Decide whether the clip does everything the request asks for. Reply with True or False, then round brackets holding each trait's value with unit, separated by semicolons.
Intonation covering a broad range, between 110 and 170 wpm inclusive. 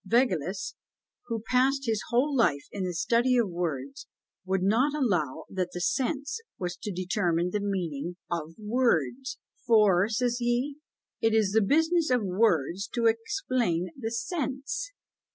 True (5.9 semitones; 145 wpm)